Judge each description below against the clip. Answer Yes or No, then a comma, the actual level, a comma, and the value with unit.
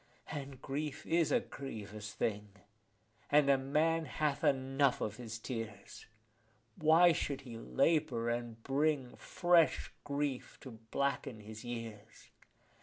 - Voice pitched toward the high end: No, low, 135 Hz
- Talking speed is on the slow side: Yes, slow, 120 wpm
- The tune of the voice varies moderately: Yes, average, 4.6 semitones